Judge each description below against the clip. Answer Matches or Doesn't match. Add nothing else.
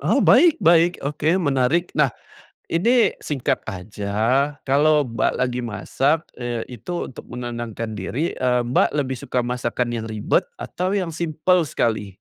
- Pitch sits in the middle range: Doesn't match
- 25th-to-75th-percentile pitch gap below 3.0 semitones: Doesn't match